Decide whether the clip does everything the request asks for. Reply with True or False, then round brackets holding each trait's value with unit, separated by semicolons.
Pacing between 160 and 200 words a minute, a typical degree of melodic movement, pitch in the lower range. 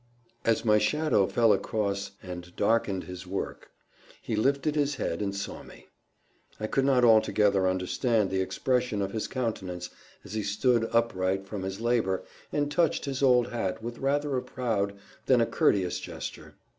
True (165 wpm; 4.4 semitones; 110 Hz)